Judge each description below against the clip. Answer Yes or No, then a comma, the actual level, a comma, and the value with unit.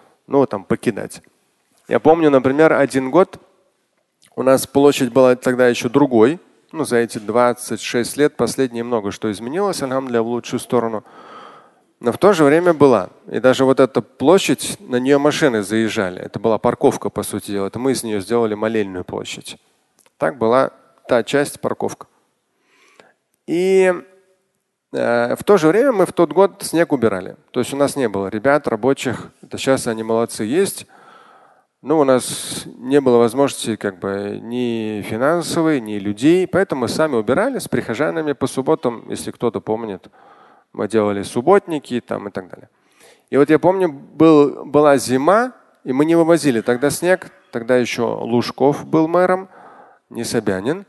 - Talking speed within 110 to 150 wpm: No, fast, 160 wpm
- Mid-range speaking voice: No, low, 130 Hz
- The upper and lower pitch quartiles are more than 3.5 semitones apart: Yes, average, 5.1 semitones